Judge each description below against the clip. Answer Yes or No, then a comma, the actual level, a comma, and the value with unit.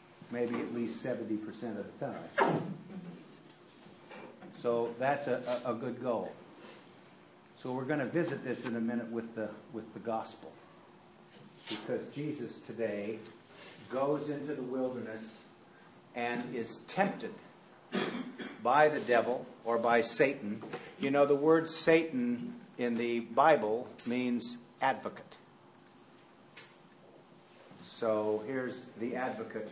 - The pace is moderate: No, slow, 115 wpm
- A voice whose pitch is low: Yes, low, 125 Hz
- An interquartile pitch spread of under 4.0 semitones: No, average, 4.3 semitones